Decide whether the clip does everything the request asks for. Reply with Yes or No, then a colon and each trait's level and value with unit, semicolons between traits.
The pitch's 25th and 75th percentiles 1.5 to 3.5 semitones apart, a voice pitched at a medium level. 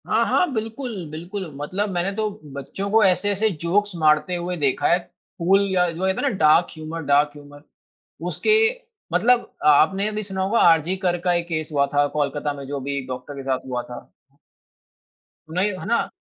No: average, 5.3 semitones; medium, 170 Hz